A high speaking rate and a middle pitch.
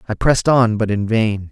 No: fast, 240 wpm; low, 110 Hz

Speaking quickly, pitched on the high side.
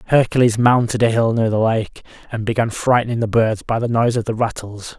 No: fast, 215 wpm; low, 115 Hz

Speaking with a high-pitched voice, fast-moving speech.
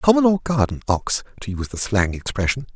No: low, 125 Hz; fast, 220 wpm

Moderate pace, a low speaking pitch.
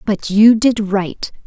No: average, 165 wpm; high, 205 Hz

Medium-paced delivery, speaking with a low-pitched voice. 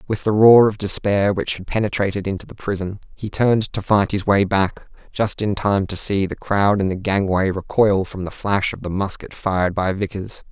No: fast, 215 wpm; low, 100 Hz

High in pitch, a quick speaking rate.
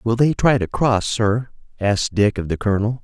No: low, 110 Hz; fast, 215 wpm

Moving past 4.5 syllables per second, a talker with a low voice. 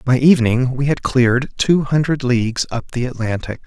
Yes: 5.3 syllables/s; low, 130 Hz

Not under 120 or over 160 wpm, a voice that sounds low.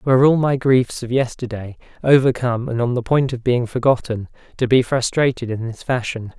No: average, 190 wpm; low, 125 Hz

